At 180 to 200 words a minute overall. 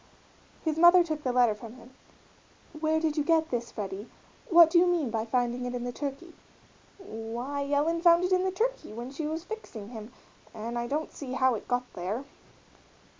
Yes: average, 195 wpm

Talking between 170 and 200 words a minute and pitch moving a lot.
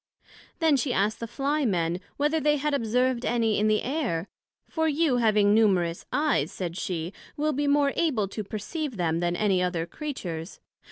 Yes: average, 175 wpm; wide, 7.8 semitones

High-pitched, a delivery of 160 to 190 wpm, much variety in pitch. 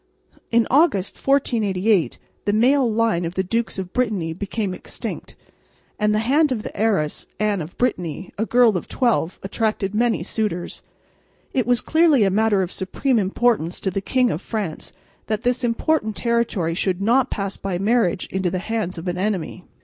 No: high, 210 Hz; average, 170 wpm; average, 4.1 semitones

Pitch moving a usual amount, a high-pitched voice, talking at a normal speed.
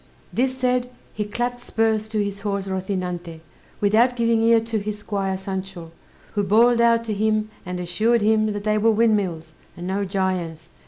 Yes: average, 3.1 semitones; high, 210 Hz; average, 170 wpm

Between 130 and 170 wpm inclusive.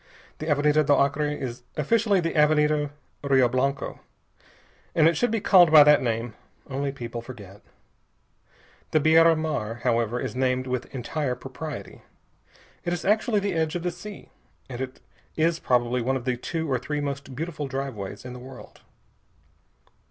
Yes: average, 160 wpm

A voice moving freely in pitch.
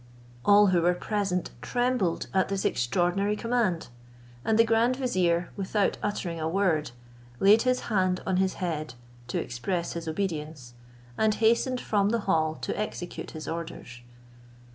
No: average, 4.1 semitones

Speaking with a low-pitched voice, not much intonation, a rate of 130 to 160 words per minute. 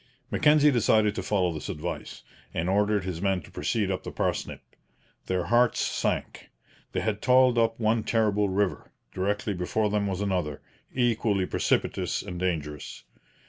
No: low, 100 Hz; average, 3.4 semitones; average, 150 wpm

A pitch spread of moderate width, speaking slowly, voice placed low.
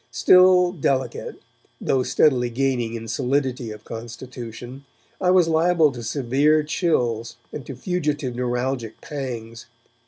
Yes: average, 4.2 semitones; slow, 120 wpm; low, 130 Hz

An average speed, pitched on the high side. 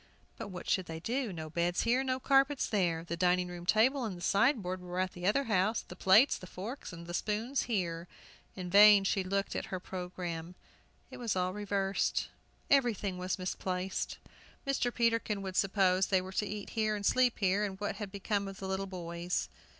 Yes: average, 190 wpm; high, 195 Hz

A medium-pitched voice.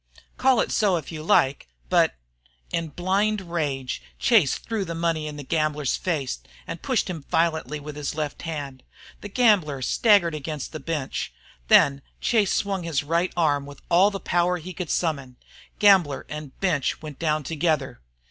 Yes: medium, 160 Hz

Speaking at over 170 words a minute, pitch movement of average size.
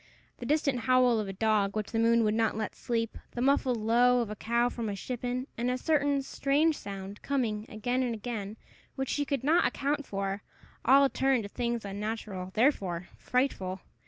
Yes: average, 190 wpm; average, 3.6 semitones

